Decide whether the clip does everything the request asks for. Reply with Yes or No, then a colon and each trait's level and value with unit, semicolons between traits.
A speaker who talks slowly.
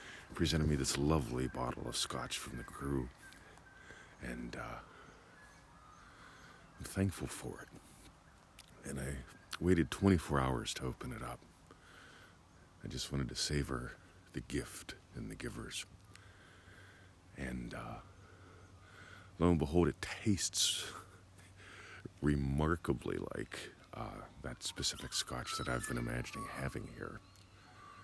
Yes: slow, 115 wpm